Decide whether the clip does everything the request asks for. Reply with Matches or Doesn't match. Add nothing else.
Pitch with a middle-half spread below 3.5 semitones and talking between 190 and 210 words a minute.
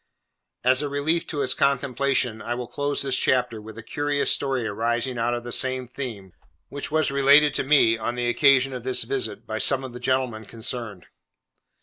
Matches